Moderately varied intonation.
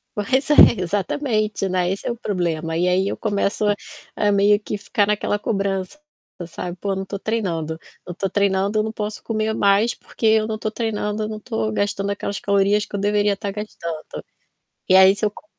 No: narrow, 1.9 semitones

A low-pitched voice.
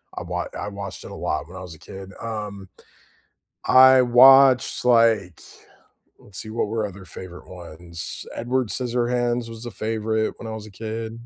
Yes: low, 110 Hz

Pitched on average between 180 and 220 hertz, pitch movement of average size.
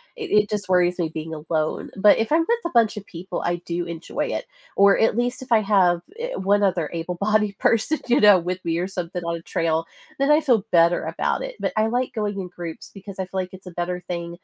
Yes: high, 190 Hz; average, 4.0 semitones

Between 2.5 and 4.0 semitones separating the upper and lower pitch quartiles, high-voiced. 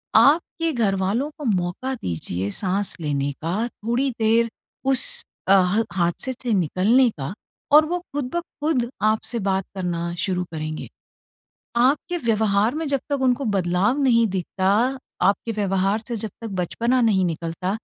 No: wide, 5.6 semitones; high, 210 Hz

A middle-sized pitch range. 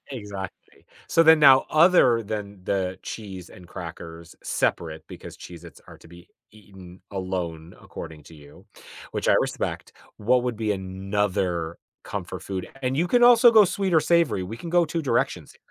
No: wide, 7.2 semitones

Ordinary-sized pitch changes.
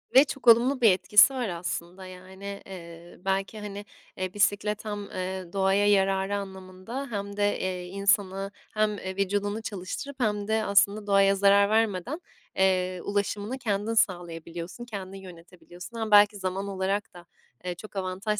No: narrow, 2.0 semitones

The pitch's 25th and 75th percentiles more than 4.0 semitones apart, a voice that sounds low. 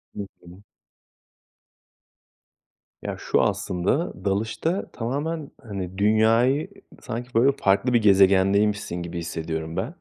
Yes: average, 4.6 semitones; low, 105 Hz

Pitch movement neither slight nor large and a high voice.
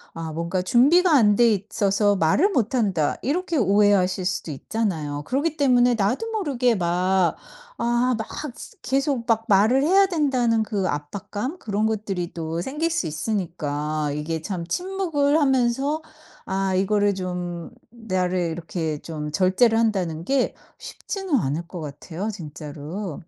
No: wide, 6.7 semitones; high, 205 Hz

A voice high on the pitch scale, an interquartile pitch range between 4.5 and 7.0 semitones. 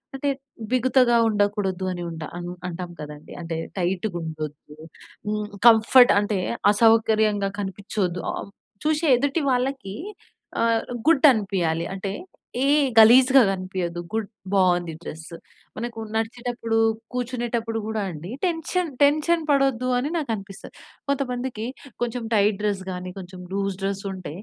Yes: high, 215 Hz; average, 4.8 semitones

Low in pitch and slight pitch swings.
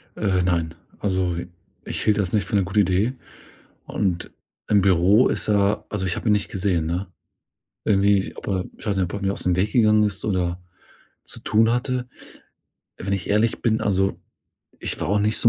Yes: low, 100 Hz; narrow, 2.3 semitones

